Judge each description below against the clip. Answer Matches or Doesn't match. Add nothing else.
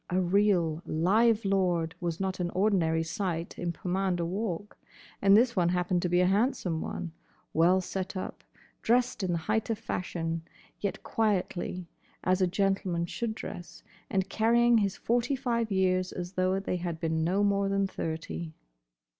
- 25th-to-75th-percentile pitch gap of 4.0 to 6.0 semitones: Doesn't match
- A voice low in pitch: Doesn't match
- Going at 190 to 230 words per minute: Doesn't match